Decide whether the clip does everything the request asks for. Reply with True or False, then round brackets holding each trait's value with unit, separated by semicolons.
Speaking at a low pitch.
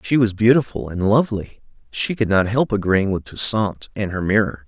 True (105 Hz)